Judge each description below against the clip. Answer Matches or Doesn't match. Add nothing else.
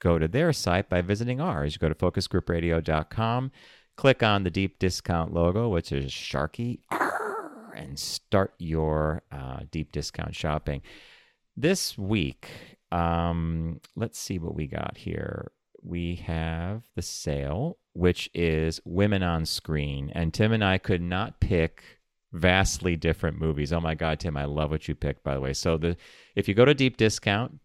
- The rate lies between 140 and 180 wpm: Matches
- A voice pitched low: Matches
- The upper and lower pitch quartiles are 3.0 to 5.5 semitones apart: Matches